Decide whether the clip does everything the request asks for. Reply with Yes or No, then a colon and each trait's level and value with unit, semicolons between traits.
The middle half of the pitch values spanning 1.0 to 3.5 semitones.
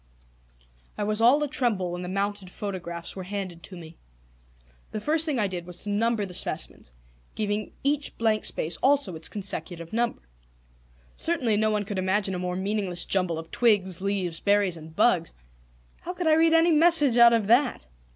No: average, 4.7 semitones